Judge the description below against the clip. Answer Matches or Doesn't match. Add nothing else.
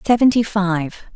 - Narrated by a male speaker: Doesn't match